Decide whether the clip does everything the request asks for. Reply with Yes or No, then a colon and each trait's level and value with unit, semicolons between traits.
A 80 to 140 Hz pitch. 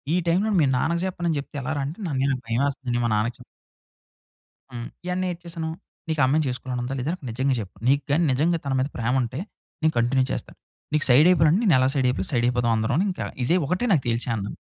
Yes: low, 135 Hz